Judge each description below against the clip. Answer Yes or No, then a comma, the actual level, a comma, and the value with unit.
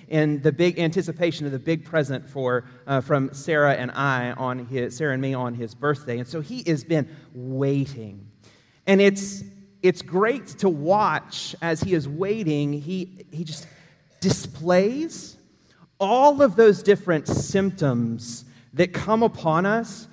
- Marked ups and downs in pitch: Yes, wide, 5.7 semitones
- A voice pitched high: No, medium, 155 Hz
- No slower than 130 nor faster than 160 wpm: Yes, average, 150 wpm